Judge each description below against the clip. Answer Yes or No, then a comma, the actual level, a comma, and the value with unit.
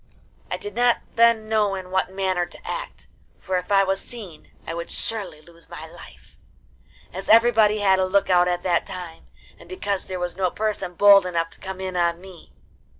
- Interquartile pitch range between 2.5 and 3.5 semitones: Yes, average, 2.9 semitones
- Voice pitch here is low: No, high, 190 Hz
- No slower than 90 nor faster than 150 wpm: No, average, 200 wpm